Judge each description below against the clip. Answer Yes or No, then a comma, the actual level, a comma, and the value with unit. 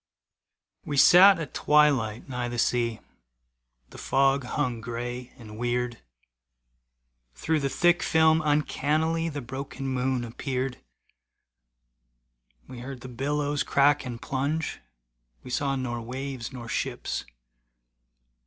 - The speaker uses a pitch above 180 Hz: No, low, 135 Hz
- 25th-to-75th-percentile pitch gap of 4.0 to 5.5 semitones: No, average, 3.2 semitones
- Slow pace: Yes, slow, 115 wpm